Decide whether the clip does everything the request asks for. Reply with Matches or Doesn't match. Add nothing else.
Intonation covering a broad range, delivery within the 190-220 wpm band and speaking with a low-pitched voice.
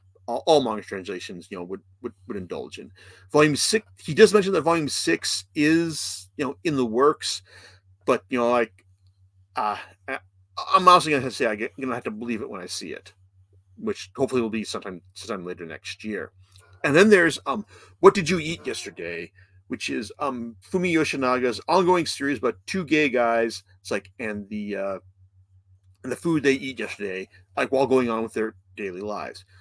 Matches